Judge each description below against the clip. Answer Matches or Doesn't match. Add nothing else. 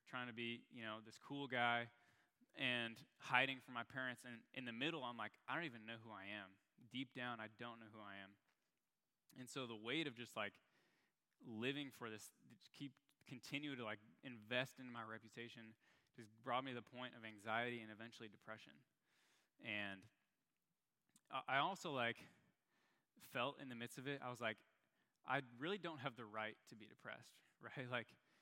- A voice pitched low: Matches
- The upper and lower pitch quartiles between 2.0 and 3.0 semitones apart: Matches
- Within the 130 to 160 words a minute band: Doesn't match